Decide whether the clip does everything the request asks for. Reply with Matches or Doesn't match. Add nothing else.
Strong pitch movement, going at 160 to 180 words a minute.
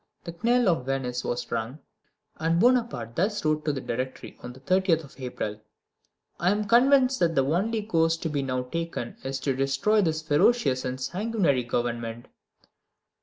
Matches